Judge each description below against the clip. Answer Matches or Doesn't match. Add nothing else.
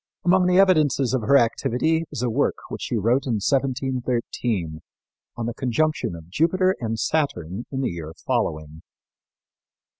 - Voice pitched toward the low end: Matches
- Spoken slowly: Doesn't match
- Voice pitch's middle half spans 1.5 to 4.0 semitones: Doesn't match